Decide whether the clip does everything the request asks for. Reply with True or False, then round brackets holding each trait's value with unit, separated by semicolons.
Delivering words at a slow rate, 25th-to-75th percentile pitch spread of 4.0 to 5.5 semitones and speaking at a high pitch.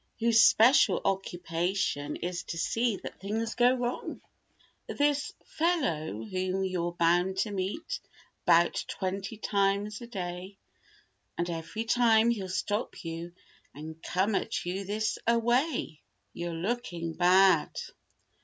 True (125 wpm; 4.6 semitones; 195 Hz)